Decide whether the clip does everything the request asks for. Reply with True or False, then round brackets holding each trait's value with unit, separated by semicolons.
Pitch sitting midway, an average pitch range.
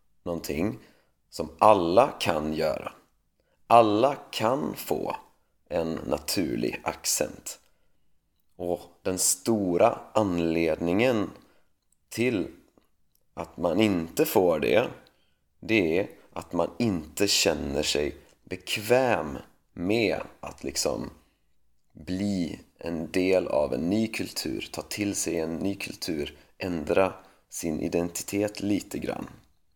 False (90 Hz; 3.4 semitones)